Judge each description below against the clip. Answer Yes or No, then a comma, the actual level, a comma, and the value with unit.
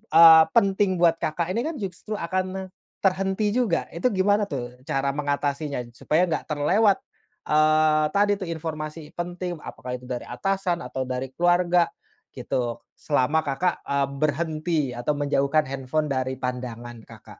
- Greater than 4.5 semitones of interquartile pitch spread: Yes, average, 5.0 semitones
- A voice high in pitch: No, medium, 155 Hz